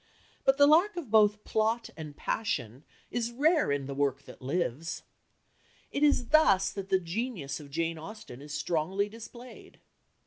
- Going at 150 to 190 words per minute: Yes, average, 160 wpm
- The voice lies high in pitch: Yes, high, 195 Hz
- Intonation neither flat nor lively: No, wide, 8.1 semitones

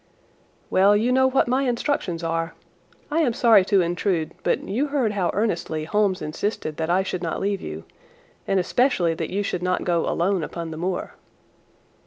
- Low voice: No, high, 190 Hz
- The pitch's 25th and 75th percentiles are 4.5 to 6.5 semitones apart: Yes, average, 4.9 semitones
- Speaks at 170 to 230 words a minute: Yes, average, 180 wpm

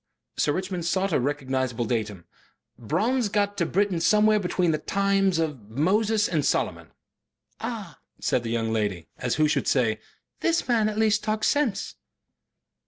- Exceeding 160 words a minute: No, average, 155 wpm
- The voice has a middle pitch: Yes, medium, 175 Hz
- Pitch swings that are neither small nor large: No, wide, 8.5 semitones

